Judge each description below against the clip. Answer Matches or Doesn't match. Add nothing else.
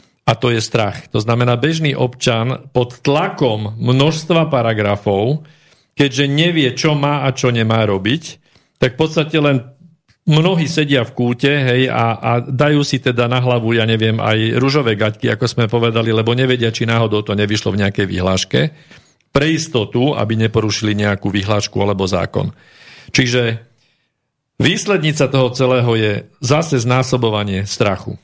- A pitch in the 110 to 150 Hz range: Matches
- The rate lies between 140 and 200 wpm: Matches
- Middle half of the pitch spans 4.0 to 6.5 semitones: Matches